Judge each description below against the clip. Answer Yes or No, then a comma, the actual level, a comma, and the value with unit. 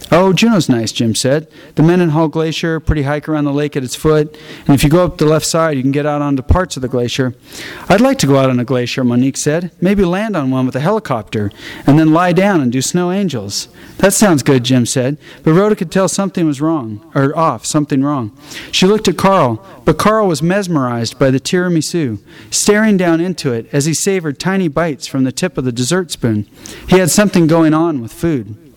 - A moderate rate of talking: No, fast, 225 wpm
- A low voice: No, medium, 155 Hz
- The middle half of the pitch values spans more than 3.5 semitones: Yes, average, 5.1 semitones